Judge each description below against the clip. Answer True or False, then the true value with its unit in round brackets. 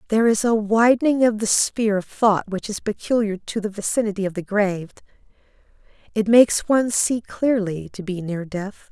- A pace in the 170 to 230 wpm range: True (180 wpm)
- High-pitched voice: True (210 Hz)